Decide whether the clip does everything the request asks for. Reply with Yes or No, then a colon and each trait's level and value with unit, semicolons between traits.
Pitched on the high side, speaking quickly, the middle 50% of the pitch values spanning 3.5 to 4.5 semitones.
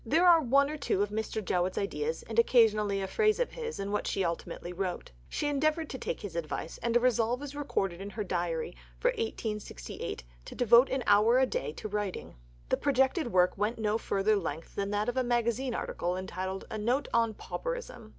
No: high, 225 Hz; fast, 210 wpm; wide, 5.6 semitones